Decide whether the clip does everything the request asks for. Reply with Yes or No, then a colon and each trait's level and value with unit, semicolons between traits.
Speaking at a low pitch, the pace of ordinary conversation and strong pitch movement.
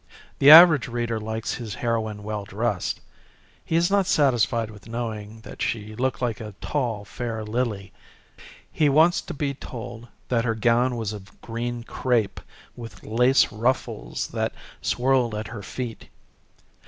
No: low, 115 Hz; average, 150 wpm; average, 2.7 semitones